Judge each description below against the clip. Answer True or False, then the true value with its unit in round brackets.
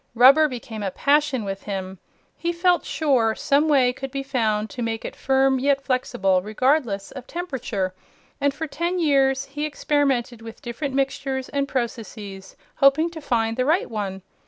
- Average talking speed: True (165 wpm)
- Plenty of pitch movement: False (4.2 semitones)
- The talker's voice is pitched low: False (265 Hz)